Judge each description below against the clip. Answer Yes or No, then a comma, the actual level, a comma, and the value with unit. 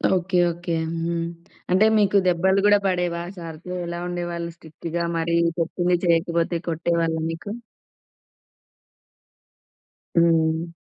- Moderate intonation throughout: No, narrow, 1.2 semitones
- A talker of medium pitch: Yes, medium, 170 Hz